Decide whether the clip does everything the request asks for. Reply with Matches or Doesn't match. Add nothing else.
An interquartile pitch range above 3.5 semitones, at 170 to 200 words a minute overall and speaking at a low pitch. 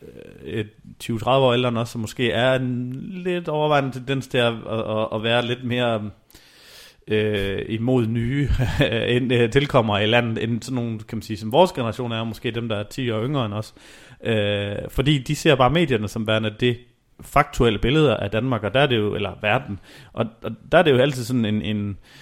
Doesn't match